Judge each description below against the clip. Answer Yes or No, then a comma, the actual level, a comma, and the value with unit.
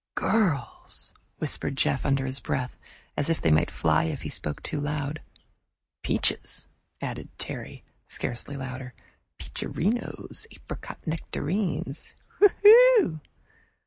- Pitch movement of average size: No, wide, 6.8 semitones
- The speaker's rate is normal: No, slow, 105 wpm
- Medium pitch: Yes, medium, 145 Hz